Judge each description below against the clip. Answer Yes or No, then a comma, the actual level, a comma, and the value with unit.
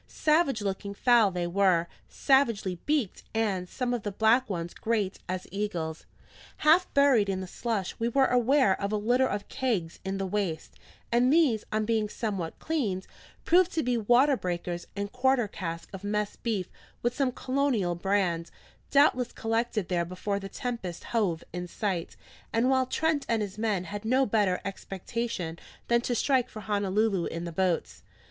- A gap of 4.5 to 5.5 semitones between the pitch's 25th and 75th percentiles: Yes, average, 4.8 semitones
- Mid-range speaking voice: No, high, 210 Hz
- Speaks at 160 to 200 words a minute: Yes, average, 170 wpm